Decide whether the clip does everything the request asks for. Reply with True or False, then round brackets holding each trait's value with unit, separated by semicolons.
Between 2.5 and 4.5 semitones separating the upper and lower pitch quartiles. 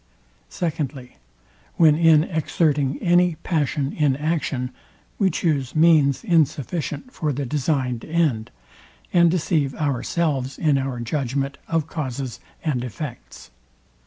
True (3.5 semitones)